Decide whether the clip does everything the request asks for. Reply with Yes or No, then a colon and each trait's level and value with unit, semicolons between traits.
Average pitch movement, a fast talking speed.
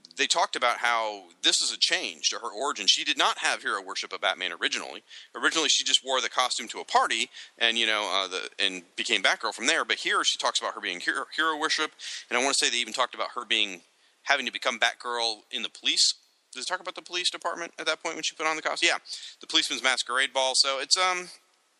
No: wide, 6.4 semitones; fast, 250 wpm